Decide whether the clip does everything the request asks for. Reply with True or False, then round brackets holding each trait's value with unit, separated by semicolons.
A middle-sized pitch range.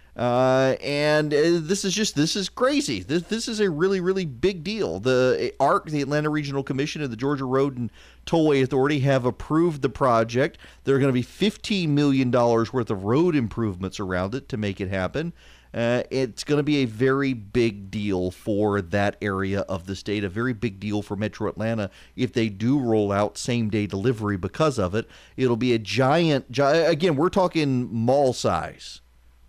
False (5.9 semitones)